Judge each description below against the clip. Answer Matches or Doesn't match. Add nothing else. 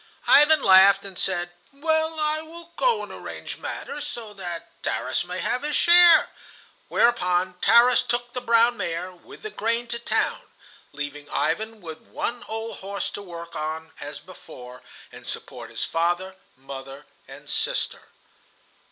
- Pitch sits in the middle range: Doesn't match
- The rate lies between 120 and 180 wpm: Matches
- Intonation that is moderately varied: Doesn't match